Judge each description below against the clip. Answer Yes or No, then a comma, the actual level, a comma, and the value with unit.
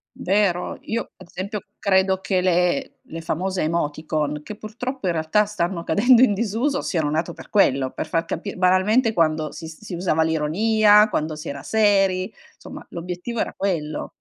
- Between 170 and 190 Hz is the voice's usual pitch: Yes, medium, 185 Hz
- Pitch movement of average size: Yes, average, 4.6 semitones